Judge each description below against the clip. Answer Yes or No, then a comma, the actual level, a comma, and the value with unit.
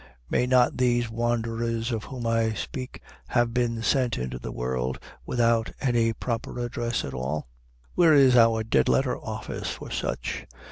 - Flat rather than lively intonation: Yes, narrow, 1.7 semitones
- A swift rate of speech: No, average, 155 wpm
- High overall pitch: No, low, 115 Hz